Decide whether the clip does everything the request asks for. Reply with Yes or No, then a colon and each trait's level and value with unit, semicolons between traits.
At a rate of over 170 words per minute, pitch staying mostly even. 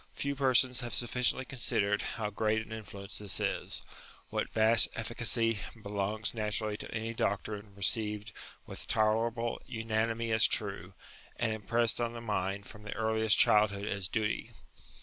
No: average, 150 wpm; narrow, 1.9 semitones